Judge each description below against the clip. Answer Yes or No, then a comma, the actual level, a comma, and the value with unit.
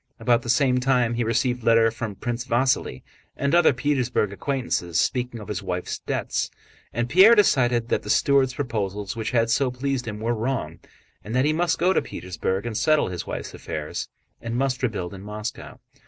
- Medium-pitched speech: No, low, 120 Hz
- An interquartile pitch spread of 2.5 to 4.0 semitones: Yes, average, 3.7 semitones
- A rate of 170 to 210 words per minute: Yes, average, 185 wpm